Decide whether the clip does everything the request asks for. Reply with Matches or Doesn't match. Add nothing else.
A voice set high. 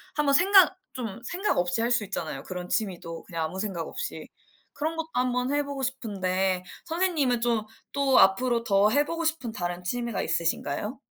Matches